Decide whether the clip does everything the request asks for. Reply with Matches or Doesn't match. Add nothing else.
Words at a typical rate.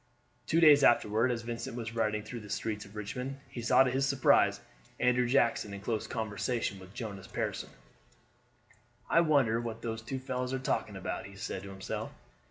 Matches